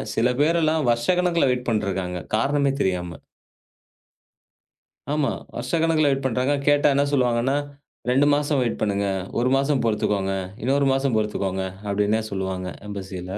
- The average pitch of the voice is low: Yes, low, 125 Hz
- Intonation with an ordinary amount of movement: No, wide, 6.1 semitones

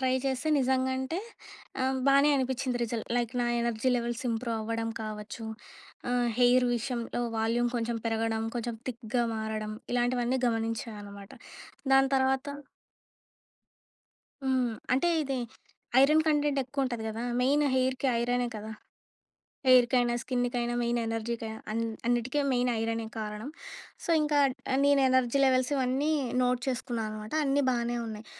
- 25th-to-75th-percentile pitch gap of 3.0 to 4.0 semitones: No, narrow, 2.5 semitones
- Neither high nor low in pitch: No, high, 245 Hz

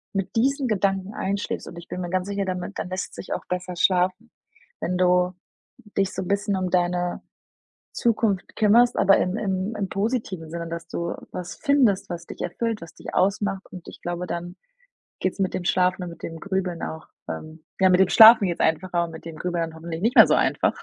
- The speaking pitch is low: No, medium, 185 Hz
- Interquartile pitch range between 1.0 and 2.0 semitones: No, narrow, 2.4 semitones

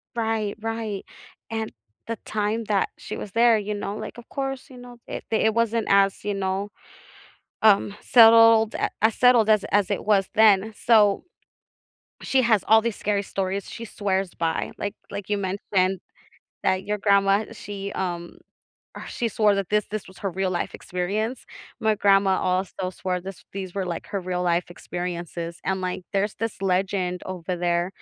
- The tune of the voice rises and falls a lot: No, average, 2.8 semitones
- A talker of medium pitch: No, high, 200 Hz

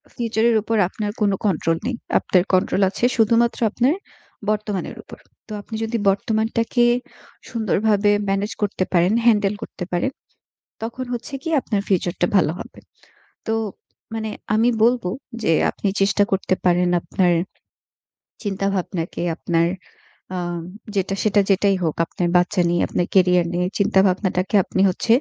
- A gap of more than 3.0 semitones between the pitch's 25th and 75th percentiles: Yes, average, 3.5 semitones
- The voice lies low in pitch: No, high, 200 Hz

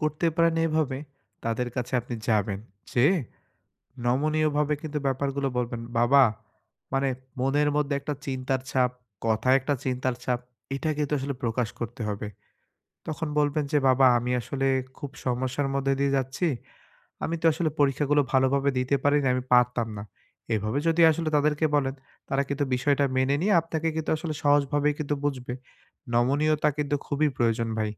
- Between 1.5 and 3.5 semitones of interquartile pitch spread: Yes, average, 2.9 semitones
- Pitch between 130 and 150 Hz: Yes, low, 135 Hz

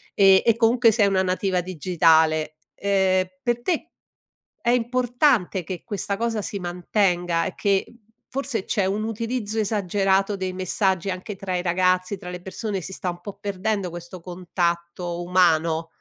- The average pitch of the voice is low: No, high, 190 Hz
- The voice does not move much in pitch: No, average, 3.1 semitones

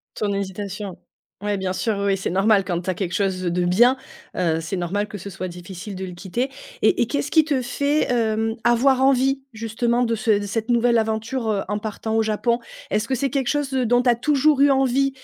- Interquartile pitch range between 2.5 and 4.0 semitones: No, average, 4.6 semitones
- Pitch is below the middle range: No, high, 220 Hz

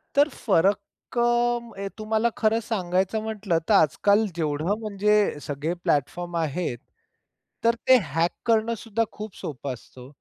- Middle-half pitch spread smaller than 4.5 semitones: No, average, 5.2 semitones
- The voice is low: No, high, 200 Hz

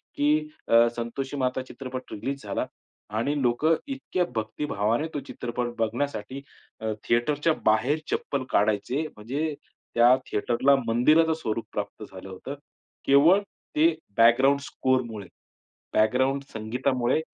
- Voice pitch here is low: Yes, low, 130 Hz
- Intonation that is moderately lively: Yes, average, 4.0 semitones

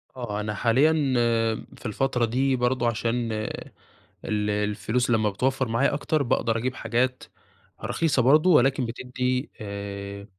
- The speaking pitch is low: Yes, low, 120 Hz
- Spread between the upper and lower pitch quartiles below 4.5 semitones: Yes, average, 3.4 semitones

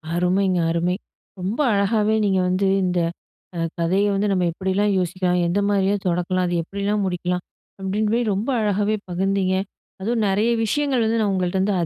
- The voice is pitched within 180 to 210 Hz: Yes, high, 195 Hz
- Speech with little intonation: Yes, narrow, 2.3 semitones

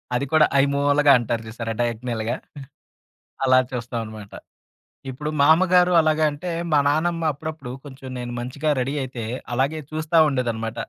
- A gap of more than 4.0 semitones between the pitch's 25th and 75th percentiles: Yes, average, 4.4 semitones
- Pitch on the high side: No, low, 135 Hz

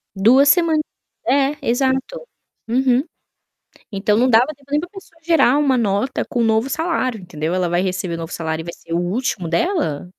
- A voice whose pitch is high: Yes, high, 240 Hz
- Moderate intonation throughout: No, wide, 7.5 semitones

